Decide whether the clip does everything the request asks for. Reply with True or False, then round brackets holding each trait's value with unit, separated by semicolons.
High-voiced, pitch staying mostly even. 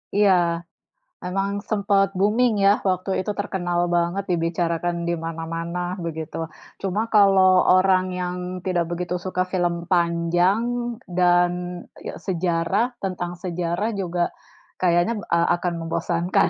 False (180 Hz; 2.1 semitones)